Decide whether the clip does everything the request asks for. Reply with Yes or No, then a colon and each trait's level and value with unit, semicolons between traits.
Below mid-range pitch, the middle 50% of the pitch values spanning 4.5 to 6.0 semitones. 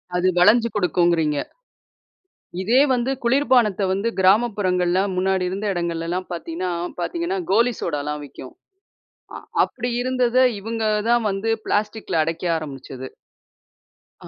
No: high, 190 Hz; average, 5.1 semitones